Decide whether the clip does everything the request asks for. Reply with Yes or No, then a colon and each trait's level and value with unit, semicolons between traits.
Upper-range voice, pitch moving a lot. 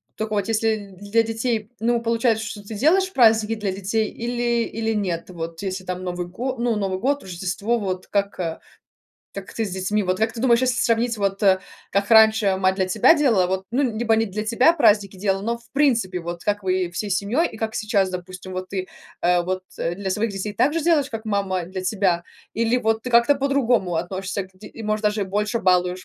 No: high, 210 Hz; average, 3.6 semitones